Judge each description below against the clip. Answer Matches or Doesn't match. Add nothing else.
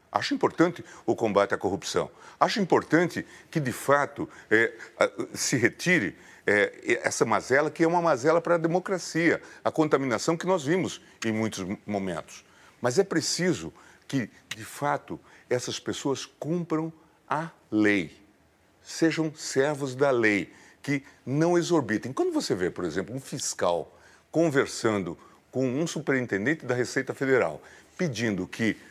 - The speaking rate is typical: Matches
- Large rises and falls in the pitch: Matches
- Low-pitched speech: Doesn't match